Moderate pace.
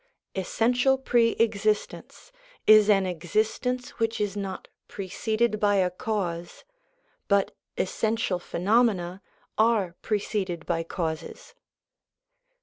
No: slow, 100 wpm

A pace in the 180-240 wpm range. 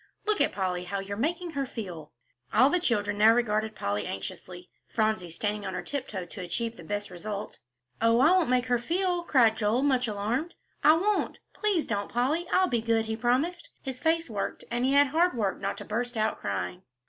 Yes: average, 200 wpm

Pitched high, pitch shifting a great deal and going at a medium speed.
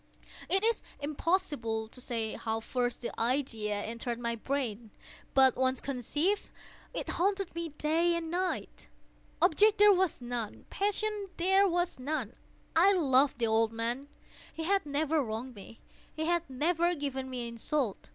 Yes: very high, 280 Hz; wide, 6.6 semitones; average, 150 wpm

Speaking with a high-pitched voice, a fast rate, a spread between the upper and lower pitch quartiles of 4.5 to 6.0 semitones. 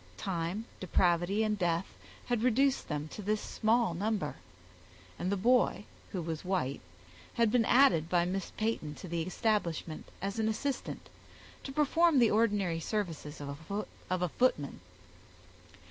No: high, 195 Hz; average, 140 wpm; average, 4.9 semitones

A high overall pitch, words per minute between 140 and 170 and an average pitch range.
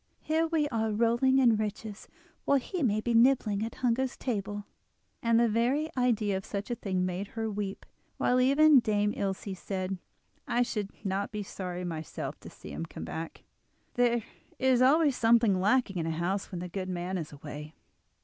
No: high, 215 Hz; average, 180 wpm; average, 4.5 semitones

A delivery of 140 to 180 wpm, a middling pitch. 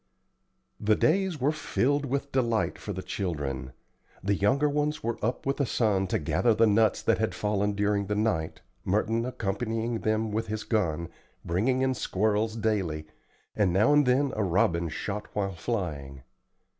No: average, 165 wpm; low, 110 Hz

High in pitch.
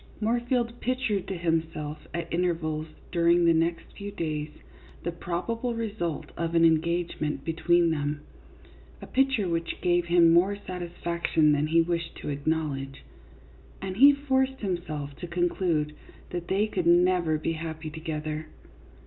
No: medium, 170 Hz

